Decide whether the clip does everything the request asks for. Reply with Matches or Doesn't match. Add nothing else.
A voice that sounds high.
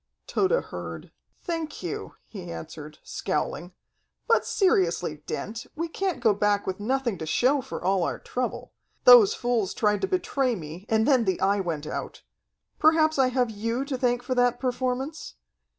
Matches